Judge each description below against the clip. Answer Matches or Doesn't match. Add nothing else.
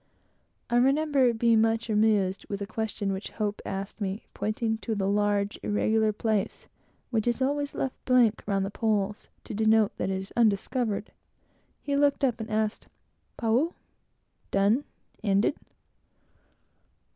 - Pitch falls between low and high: Doesn't match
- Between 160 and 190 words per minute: Doesn't match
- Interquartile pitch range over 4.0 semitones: Doesn't match